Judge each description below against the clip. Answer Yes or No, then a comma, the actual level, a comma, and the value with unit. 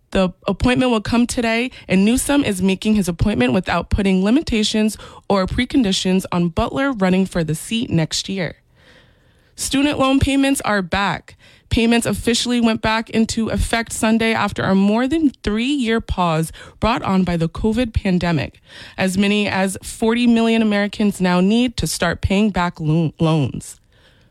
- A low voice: No, high, 205 Hz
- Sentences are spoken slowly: No, average, 155 wpm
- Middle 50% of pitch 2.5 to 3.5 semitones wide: No, average, 4.5 semitones